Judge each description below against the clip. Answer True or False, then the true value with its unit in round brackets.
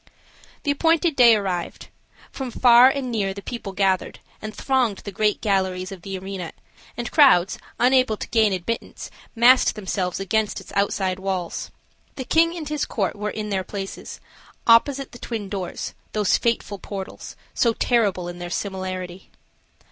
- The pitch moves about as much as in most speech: True (4.2 semitones)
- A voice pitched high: True (210 Hz)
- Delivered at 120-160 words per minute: True (155 wpm)